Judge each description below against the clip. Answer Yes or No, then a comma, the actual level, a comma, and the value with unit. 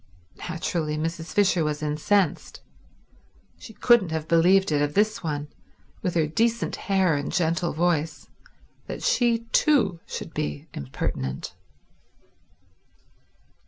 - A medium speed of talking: No, slow, 115 wpm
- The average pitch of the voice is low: No, medium, 165 Hz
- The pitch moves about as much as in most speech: Yes, average, 4.3 semitones